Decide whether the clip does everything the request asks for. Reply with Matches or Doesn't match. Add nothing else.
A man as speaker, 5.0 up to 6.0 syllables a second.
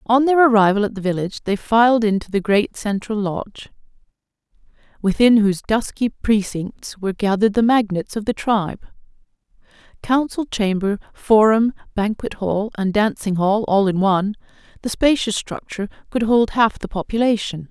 Doesn't match